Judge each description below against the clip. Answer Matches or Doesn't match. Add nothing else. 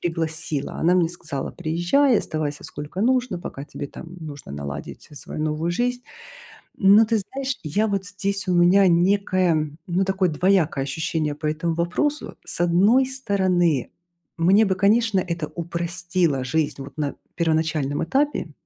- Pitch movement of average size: Matches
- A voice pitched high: Doesn't match